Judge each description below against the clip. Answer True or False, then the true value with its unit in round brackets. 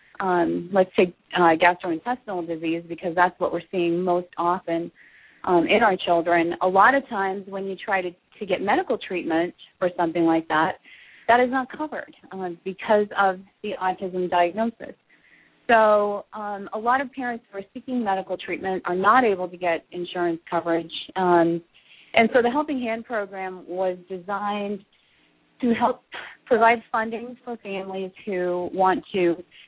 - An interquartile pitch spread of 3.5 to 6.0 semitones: True (4.1 semitones)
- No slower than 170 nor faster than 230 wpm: False (160 wpm)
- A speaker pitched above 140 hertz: True (190 Hz)